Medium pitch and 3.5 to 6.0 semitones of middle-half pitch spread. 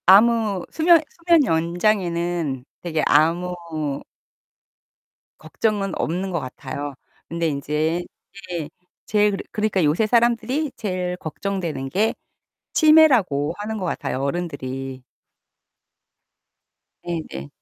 Yes: medium, 175 Hz; wide, 5.6 semitones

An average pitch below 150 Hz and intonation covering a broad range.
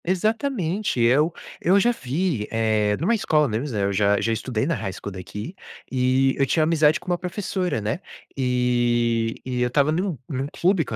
Yes: low, 135 Hz; wide, 7.2 semitones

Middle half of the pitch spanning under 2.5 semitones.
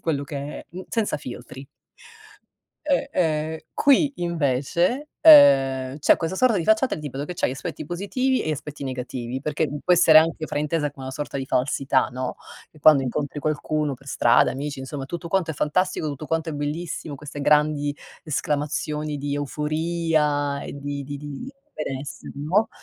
No: average, 2.9 semitones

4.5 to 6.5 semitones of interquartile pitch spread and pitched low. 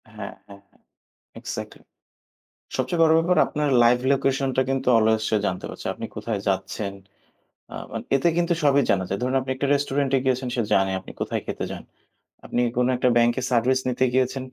No: average, 3.3 semitones; low, 130 Hz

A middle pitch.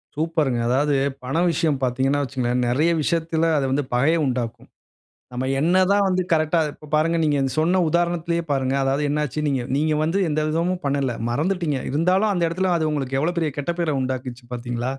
Yes: medium, 150 Hz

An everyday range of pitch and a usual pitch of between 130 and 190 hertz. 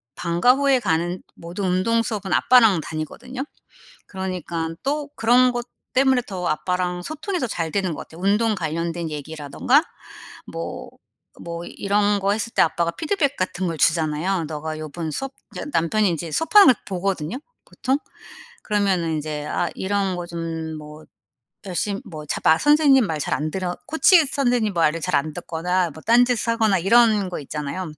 No: wide, 6.0 semitones; medium, 185 Hz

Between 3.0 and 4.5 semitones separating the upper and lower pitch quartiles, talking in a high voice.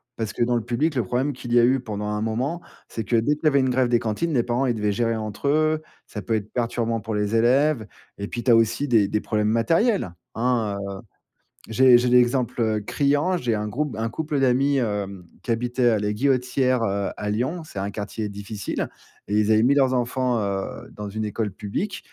No: average, 3.6 semitones; low, 120 Hz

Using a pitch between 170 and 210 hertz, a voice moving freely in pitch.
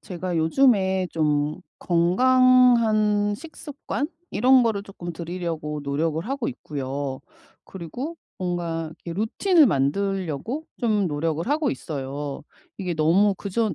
Yes: medium, 185 Hz; wide, 6.5 semitones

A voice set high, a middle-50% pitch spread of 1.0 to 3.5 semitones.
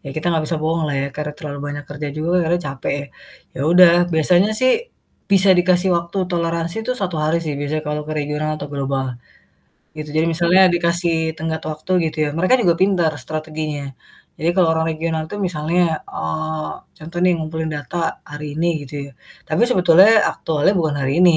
No: medium, 160 Hz; narrow, 2.4 semitones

